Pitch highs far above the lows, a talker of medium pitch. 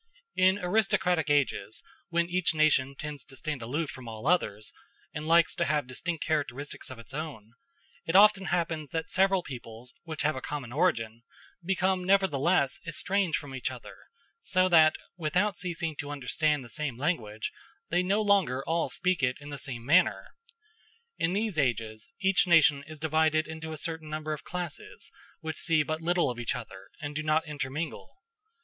No: average, 4.3 semitones; medium, 155 Hz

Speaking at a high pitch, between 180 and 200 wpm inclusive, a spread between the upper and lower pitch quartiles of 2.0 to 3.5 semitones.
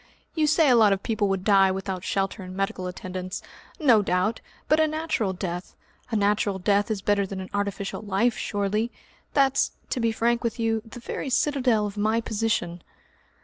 Yes: high, 205 Hz; average, 185 wpm; average, 3.2 semitones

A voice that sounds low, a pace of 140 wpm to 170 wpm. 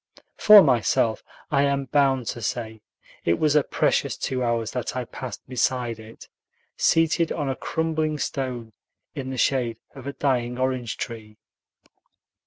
Yes: low, 130 Hz; average, 150 wpm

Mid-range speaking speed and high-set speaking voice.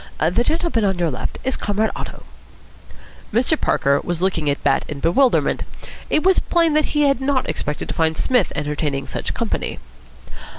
Yes: average, 170 wpm; high, 200 Hz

